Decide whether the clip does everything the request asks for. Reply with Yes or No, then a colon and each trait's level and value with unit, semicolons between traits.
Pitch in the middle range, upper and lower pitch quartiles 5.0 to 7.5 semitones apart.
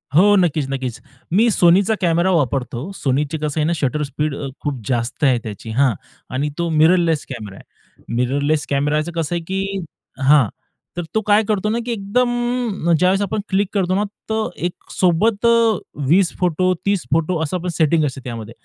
Yes: medium, 165 Hz; wide, 5.4 semitones